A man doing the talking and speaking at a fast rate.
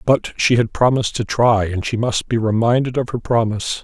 Yes: male; fast, 220 wpm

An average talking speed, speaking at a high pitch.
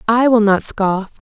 Yes: average, 190 wpm; high, 215 Hz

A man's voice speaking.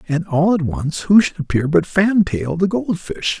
Yes: male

